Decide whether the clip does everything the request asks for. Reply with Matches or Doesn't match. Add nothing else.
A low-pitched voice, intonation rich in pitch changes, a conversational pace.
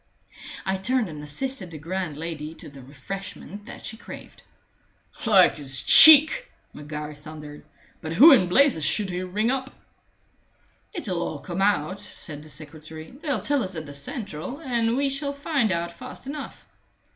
Doesn't match